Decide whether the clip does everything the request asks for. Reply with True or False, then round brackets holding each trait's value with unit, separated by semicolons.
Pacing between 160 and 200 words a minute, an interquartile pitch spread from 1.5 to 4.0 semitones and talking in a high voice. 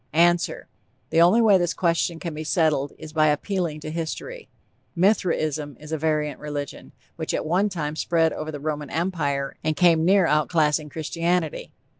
False (170 wpm; 2.4 semitones; 160 Hz)